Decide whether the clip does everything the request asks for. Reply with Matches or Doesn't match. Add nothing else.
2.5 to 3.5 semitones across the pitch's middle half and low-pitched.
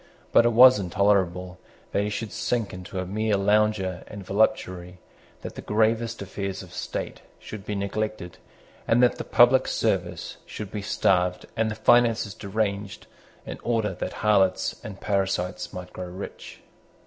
Matches